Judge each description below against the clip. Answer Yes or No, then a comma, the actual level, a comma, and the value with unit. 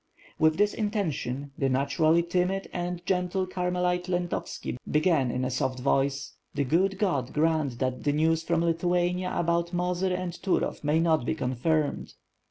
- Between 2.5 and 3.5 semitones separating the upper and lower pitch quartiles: No, average, 3.9 semitones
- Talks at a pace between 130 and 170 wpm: Yes, average, 165 wpm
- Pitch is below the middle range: No, medium, 170 Hz